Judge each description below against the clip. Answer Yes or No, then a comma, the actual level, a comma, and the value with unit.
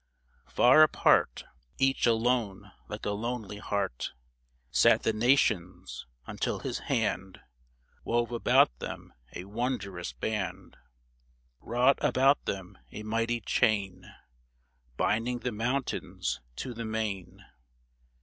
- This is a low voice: Yes, low, 110 Hz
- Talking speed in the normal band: No, slow, 110 wpm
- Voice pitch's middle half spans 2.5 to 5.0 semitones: Yes, average, 4.1 semitones